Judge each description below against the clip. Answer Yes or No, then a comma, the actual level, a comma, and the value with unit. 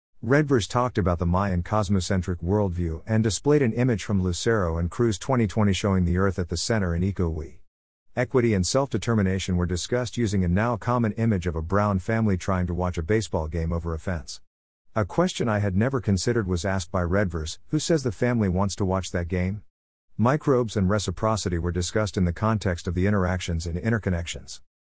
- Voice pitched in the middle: No, very low, 95 Hz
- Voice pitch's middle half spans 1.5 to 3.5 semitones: No, average, 4.2 semitones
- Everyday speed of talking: Yes, average, 190 wpm